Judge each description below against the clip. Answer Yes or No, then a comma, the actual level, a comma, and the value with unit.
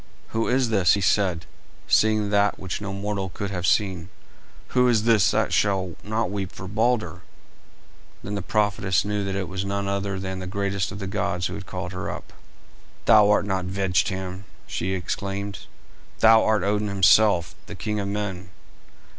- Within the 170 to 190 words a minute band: Yes, average, 175 wpm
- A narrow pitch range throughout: Yes, narrow, 1.7 semitones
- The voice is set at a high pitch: No, low, 100 Hz